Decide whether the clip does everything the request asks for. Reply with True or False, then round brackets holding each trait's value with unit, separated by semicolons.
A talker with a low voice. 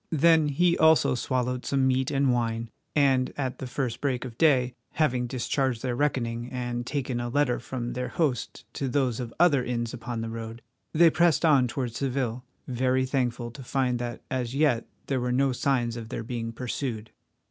True (125 Hz)